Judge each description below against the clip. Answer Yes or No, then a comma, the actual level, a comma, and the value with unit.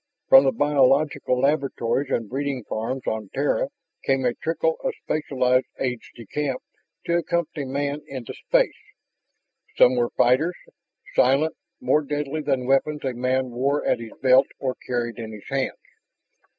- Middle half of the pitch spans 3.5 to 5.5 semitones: No, average, 2.7 semitones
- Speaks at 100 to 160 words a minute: Yes, average, 150 wpm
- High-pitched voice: No, low, 135 Hz